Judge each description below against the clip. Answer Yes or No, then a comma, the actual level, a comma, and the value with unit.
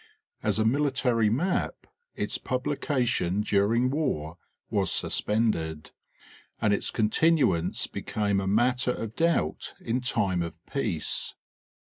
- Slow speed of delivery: Yes, slow, 115 wpm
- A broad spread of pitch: No, average, 4.7 semitones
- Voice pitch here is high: No, low, 110 Hz